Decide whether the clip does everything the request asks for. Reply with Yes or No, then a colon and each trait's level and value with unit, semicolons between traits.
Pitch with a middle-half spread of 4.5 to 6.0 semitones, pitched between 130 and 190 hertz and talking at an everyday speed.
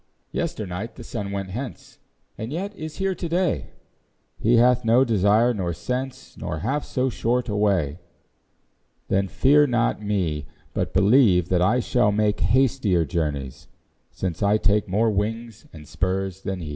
No: average, 5.1 semitones; low, 105 Hz; average, 160 wpm